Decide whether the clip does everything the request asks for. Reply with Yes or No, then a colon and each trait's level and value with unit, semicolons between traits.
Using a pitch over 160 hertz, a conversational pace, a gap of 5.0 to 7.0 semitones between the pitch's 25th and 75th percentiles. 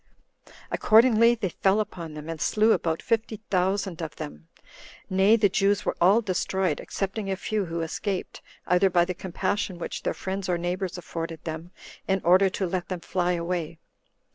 No: medium, 185 Hz; average, 170 wpm; average, 2.8 semitones